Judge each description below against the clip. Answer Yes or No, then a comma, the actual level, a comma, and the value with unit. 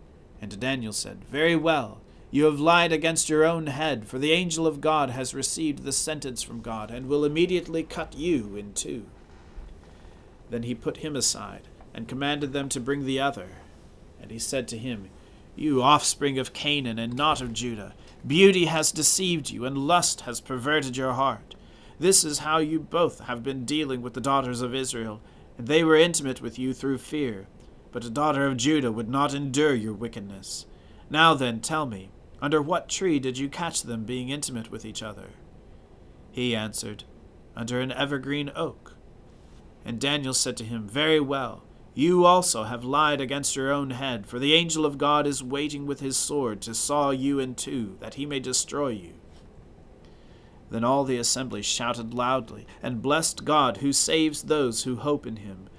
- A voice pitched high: No, low, 135 Hz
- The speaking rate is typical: Yes, average, 180 wpm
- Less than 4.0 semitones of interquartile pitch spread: No, average, 4.5 semitones